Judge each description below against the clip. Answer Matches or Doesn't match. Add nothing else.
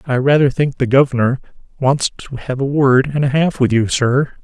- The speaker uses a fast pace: Matches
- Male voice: Matches